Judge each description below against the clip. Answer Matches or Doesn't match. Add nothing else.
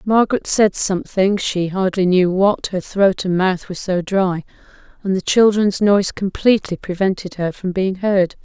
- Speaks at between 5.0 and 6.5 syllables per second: Doesn't match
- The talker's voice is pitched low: Doesn't match